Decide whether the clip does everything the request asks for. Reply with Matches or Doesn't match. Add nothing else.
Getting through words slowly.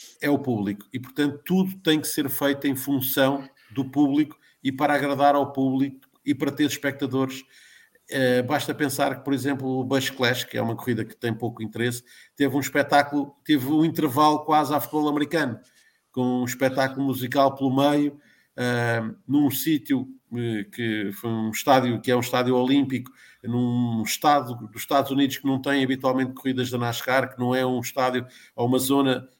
Doesn't match